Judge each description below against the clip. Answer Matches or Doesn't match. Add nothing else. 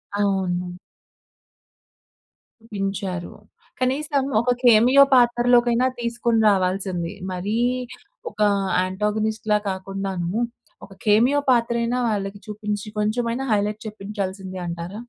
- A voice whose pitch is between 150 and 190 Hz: Doesn't match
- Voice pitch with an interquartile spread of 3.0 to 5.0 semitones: Matches